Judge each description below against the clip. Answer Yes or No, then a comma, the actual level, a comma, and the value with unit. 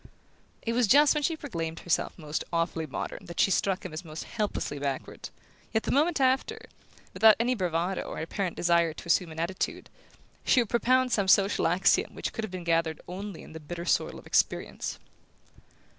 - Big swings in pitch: Yes, wide, 5.8 semitones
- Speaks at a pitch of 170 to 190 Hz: Yes, medium, 185 Hz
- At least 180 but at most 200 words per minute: Yes, average, 190 wpm